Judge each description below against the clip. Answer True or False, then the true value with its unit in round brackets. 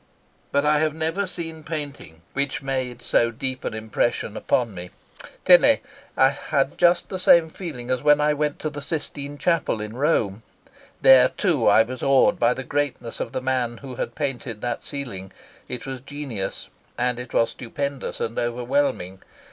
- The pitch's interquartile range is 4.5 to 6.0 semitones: False (3.8 semitones)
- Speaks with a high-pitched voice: False (135 Hz)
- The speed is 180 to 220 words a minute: False (170 wpm)